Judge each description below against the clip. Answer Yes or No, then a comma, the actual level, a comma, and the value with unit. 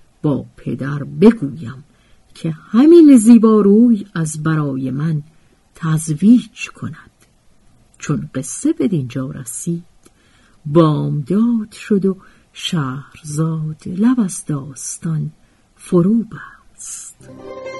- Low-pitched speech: No, medium, 165 Hz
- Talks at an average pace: No, slow, 80 wpm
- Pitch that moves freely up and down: Yes, wide, 6.8 semitones